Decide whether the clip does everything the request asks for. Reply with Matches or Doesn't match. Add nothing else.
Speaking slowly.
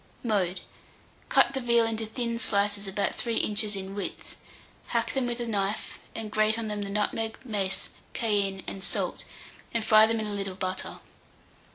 Doesn't match